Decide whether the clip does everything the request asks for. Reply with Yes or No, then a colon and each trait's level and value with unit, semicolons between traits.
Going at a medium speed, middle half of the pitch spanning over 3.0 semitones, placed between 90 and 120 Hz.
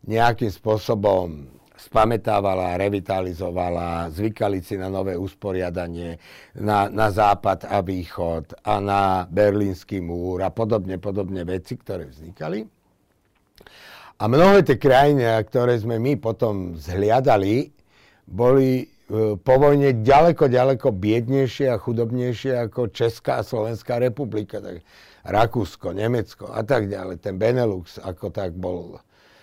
Yes: average, 120 wpm; average, 4.2 semitones; low, 100 Hz